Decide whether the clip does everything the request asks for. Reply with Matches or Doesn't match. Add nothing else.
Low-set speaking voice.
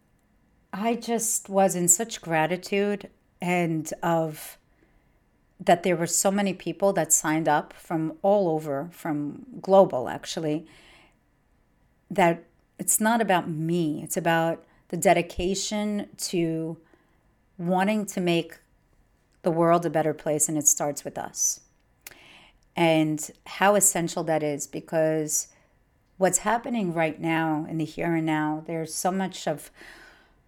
Doesn't match